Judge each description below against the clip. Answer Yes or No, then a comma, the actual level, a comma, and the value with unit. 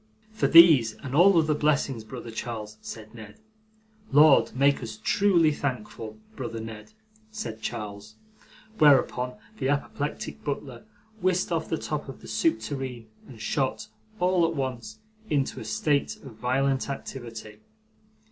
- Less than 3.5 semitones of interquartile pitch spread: No, average, 5.0 semitones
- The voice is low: Yes, low, 130 Hz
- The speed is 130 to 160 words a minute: Yes, average, 140 wpm